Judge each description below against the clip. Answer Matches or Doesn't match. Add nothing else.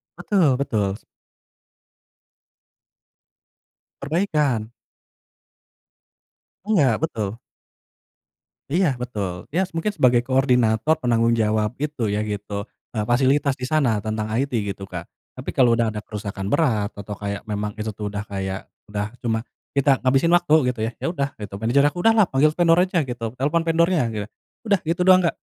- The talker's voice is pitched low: Matches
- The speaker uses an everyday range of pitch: Doesn't match